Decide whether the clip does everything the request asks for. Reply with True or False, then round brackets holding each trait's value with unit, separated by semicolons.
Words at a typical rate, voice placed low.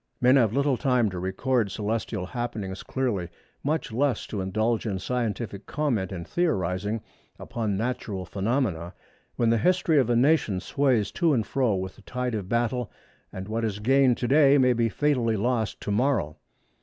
True (170 wpm; 115 Hz)